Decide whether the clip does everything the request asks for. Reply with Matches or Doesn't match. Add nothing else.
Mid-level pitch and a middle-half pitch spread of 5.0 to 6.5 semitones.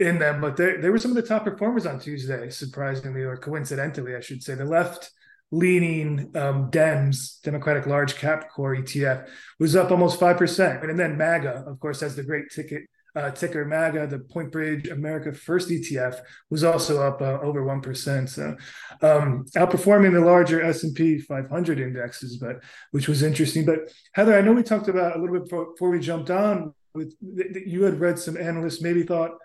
Doesn't match